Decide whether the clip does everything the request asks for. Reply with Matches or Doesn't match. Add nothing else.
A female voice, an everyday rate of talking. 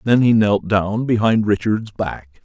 Doesn't match